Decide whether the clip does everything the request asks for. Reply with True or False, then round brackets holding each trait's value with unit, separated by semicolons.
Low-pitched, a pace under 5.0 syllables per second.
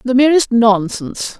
False (235 Hz; 4.7 syllables/s)